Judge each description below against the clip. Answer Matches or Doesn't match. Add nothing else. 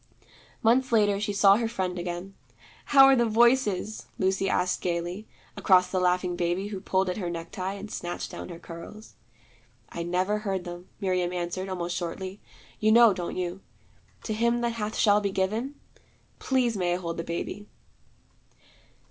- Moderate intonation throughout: Matches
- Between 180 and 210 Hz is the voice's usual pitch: Matches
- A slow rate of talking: Doesn't match